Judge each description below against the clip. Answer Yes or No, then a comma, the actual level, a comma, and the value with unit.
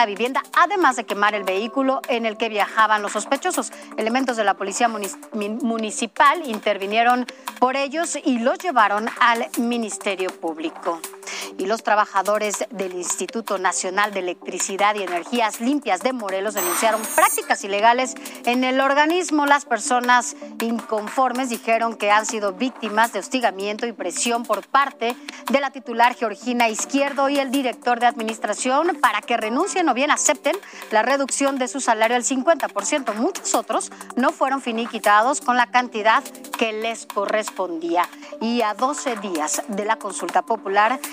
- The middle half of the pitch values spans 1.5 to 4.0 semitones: No, average, 4.4 semitones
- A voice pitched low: No, high, 235 Hz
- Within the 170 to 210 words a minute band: No, average, 150 wpm